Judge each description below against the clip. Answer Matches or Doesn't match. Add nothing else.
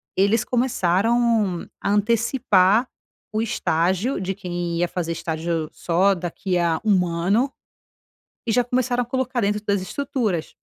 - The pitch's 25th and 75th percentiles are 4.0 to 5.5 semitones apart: Matches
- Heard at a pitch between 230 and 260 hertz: Doesn't match